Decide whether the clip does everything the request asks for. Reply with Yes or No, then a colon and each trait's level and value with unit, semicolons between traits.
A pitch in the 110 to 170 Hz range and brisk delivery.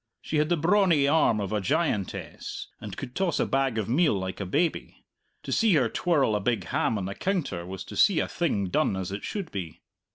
Yes: low, 135 Hz; fast, 225 wpm